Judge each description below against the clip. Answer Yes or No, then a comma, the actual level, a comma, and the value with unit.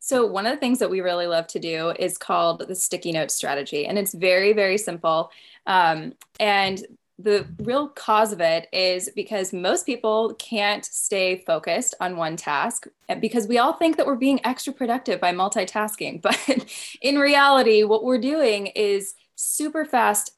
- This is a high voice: Yes, high, 210 Hz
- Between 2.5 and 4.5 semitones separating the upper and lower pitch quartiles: No, average, 5.0 semitones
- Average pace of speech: Yes, average, 175 wpm